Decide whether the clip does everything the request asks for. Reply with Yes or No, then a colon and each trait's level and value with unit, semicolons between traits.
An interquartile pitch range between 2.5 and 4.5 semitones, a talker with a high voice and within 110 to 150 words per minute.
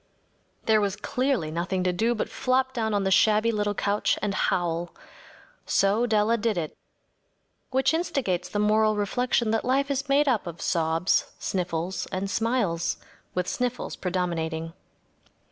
No: average, 5.0 semitones; high, 210 Hz; average, 145 wpm